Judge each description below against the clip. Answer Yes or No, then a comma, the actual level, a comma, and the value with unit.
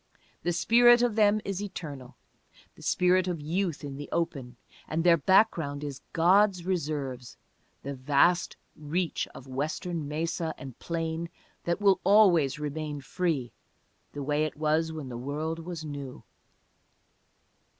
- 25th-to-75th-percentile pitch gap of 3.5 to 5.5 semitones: Yes, average, 3.9 semitones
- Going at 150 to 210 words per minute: No, average, 140 wpm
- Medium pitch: Yes, medium, 160 Hz